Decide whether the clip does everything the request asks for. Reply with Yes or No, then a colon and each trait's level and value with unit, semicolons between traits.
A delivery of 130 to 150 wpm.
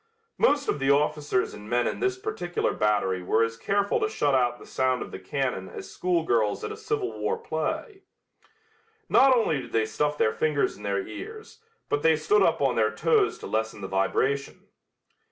No: average, 190 wpm